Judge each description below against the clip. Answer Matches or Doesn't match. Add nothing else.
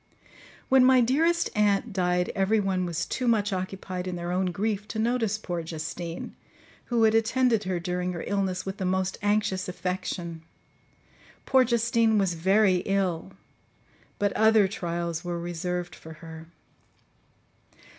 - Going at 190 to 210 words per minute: Doesn't match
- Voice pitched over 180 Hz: Matches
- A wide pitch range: Doesn't match